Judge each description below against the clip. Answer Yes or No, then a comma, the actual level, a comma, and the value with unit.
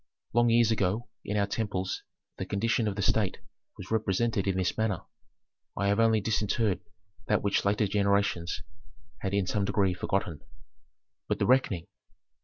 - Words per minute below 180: Yes, average, 155 wpm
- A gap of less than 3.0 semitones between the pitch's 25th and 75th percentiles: Yes, narrow, 2.4 semitones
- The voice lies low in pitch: Yes, low, 100 Hz